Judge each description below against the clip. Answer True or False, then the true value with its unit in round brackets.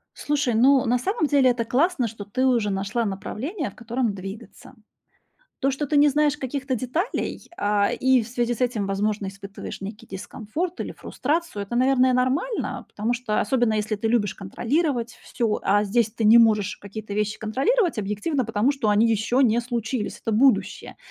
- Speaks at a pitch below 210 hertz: False (235 Hz)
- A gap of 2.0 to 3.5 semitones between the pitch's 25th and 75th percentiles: False (4.1 semitones)